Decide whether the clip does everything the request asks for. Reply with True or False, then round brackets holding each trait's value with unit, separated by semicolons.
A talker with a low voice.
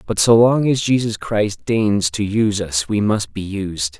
True (105 Hz)